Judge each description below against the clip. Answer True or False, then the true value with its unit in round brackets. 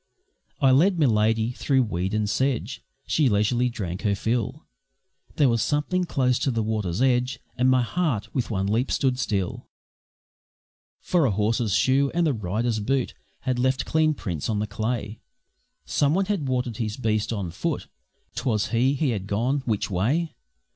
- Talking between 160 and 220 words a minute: True (165 wpm)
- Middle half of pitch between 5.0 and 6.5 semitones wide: False (4.1 semitones)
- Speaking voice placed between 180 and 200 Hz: False (120 Hz)